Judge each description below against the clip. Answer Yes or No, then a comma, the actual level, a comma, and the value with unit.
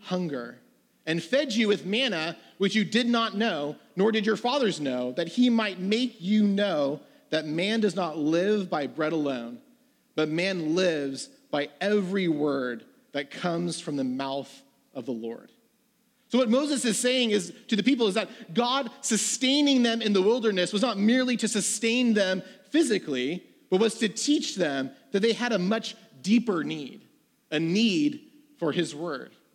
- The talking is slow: No, average, 175 wpm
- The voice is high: Yes, high, 210 Hz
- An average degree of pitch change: No, wide, 6.1 semitones